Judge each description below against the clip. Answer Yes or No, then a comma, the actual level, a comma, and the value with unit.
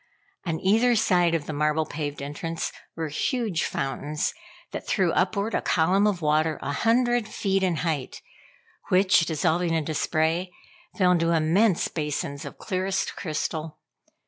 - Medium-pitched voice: Yes, medium, 165 Hz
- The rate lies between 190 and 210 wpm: No, average, 145 wpm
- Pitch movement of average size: Yes, average, 3.7 semitones